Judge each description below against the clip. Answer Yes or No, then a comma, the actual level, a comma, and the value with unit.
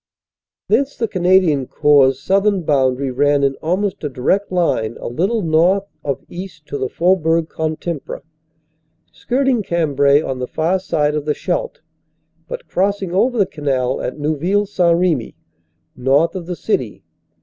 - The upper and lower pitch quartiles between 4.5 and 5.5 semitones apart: Yes, average, 5.1 semitones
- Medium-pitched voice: Yes, medium, 165 Hz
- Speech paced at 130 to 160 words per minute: Yes, average, 150 wpm